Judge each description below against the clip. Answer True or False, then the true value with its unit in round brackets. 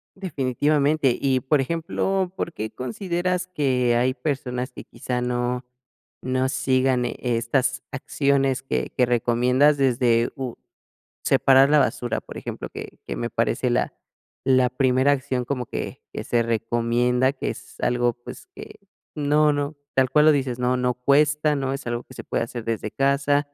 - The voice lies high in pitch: False (130 Hz)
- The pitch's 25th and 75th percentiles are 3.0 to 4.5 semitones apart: False (2.6 semitones)